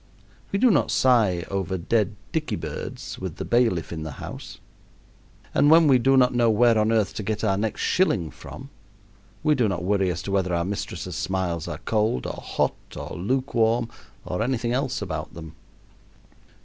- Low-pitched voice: Yes, low, 110 Hz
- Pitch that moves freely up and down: No, average, 5.0 semitones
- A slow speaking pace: No, average, 180 wpm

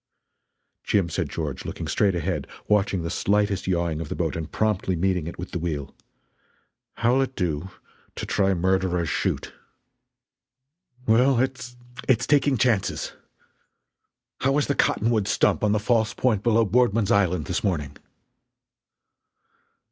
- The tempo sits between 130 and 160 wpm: Yes, average, 140 wpm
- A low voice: Yes, low, 100 Hz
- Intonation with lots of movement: No, average, 5.0 semitones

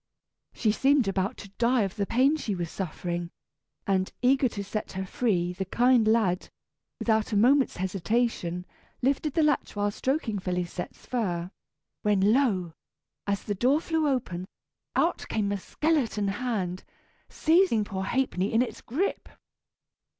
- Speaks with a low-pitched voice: No, high, 210 Hz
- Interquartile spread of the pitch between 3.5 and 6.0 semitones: Yes, average, 5.1 semitones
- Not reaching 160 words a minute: Yes, average, 145 wpm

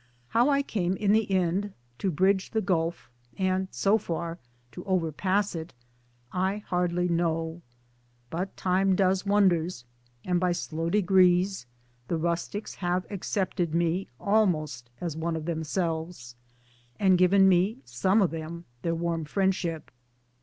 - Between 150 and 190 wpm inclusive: No, slow, 135 wpm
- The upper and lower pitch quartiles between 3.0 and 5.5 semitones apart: No, narrow, 2.6 semitones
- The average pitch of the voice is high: No, medium, 180 Hz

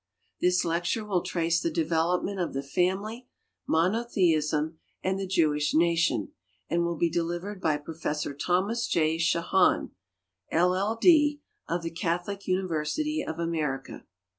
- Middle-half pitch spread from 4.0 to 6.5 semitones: No, average, 2.8 semitones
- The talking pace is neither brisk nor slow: No, slow, 130 wpm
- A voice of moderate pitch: Yes, medium, 170 Hz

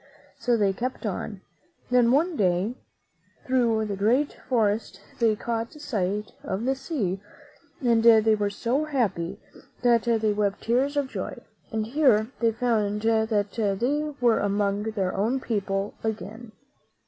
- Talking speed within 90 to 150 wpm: Yes, average, 140 wpm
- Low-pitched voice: No, high, 225 Hz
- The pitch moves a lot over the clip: No, average, 3.1 semitones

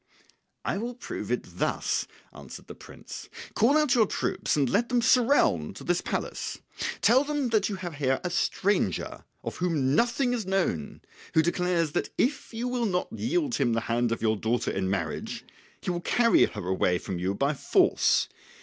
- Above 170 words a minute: Yes, average, 180 wpm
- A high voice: No, medium, 180 Hz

